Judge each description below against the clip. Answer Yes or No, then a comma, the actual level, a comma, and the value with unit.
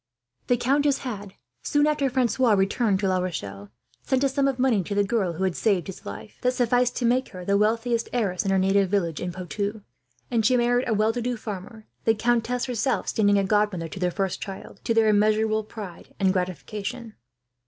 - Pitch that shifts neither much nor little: Yes, average, 4.1 semitones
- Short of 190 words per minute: No, fast, 205 wpm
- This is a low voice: No, high, 215 Hz